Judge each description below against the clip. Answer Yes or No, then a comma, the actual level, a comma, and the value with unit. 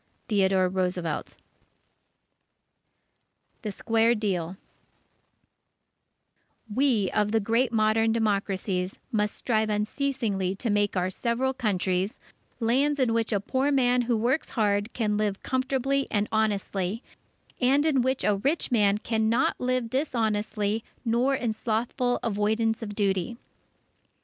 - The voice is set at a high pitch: Yes, high, 220 Hz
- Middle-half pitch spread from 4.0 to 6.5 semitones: No, average, 3.4 semitones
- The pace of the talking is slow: Yes, slow, 120 wpm